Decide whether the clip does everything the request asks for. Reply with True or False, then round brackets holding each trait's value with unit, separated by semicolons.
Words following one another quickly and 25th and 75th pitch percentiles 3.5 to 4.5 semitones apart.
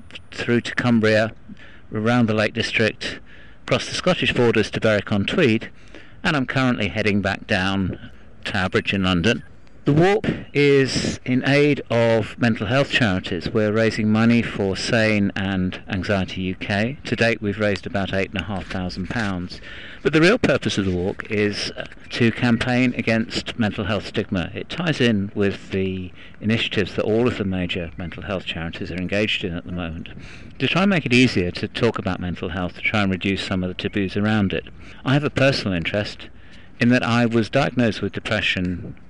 False (180 wpm; 3.9 semitones)